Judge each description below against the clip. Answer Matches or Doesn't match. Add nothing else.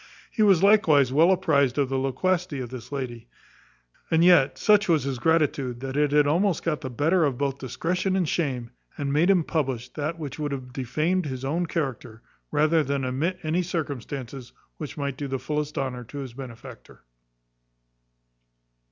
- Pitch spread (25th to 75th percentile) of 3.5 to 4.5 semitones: Matches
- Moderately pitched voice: Matches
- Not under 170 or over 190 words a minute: Matches